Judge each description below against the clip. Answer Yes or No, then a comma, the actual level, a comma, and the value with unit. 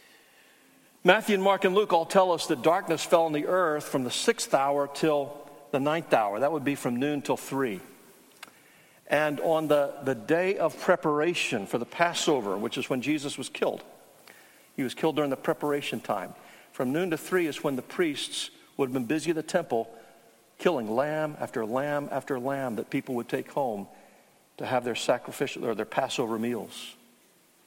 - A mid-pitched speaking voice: Yes, medium, 150 Hz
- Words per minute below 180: No, average, 185 wpm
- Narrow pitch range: No, average, 3.8 semitones